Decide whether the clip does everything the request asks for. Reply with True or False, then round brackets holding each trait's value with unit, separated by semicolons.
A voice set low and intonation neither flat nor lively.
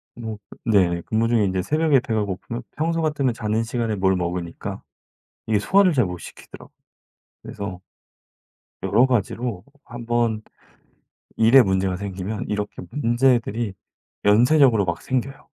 True (110 Hz; 4.3 semitones)